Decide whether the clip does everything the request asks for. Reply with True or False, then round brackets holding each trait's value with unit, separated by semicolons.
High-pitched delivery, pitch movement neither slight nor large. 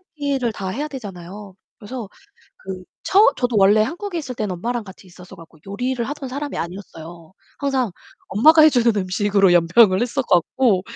False (215 Hz; 5.8 semitones)